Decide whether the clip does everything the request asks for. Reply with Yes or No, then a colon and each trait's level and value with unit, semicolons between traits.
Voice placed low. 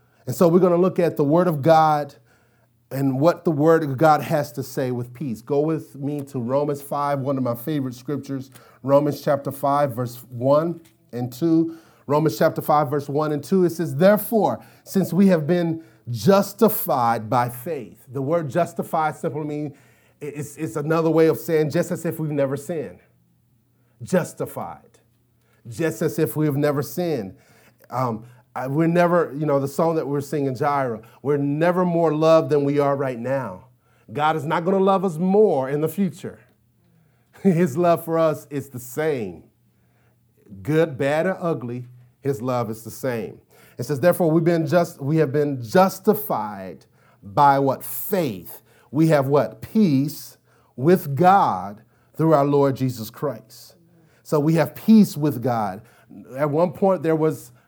No: medium, 150 Hz